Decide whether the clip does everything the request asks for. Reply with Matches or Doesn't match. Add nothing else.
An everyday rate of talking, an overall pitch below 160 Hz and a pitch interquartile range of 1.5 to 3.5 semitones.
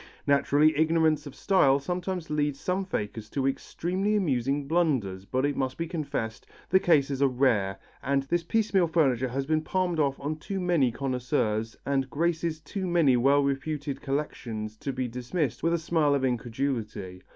Doesn't match